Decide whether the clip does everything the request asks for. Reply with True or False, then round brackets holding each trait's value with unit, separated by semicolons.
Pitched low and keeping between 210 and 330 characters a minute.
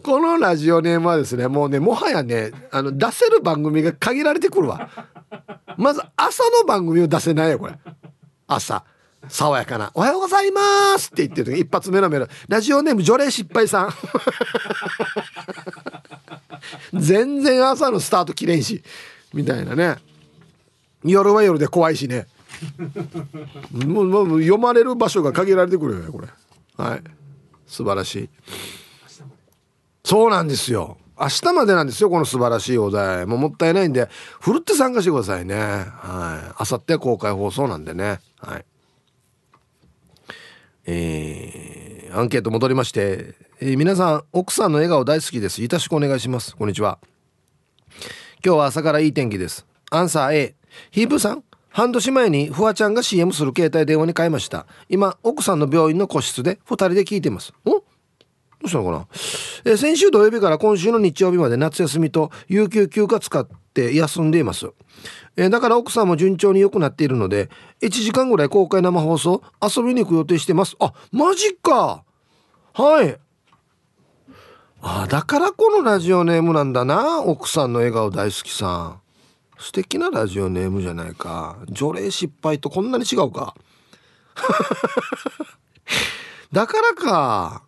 False (170 Hz; 295 characters per minute)